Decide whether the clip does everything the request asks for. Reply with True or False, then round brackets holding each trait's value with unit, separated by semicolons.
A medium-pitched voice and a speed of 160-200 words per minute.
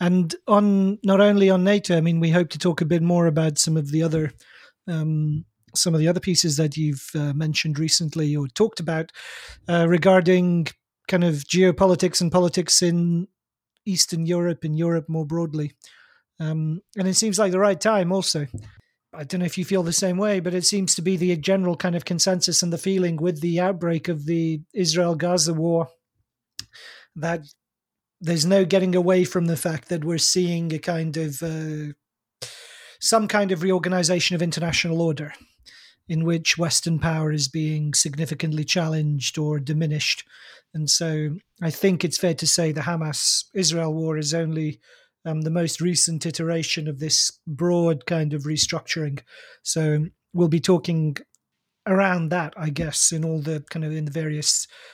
True (170 Hz; 175 wpm)